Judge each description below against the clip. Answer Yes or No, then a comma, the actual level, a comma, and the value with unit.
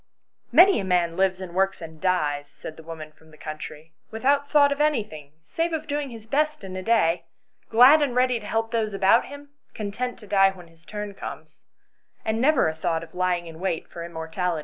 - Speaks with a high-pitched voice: Yes, high, 195 Hz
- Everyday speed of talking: No, fast, 220 wpm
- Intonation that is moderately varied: No, wide, 7.0 semitones